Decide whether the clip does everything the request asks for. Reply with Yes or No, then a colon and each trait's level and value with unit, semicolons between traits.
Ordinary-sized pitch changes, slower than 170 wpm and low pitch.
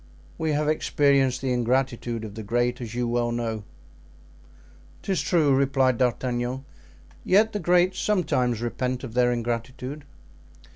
Yes: average, 3.2 semitones; slow, 135 wpm; low, 125 Hz